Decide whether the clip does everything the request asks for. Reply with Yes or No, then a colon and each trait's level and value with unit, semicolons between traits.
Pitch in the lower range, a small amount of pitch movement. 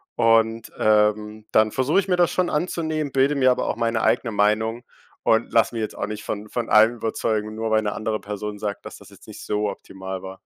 Yes: low, 110 Hz; narrow, 2.3 semitones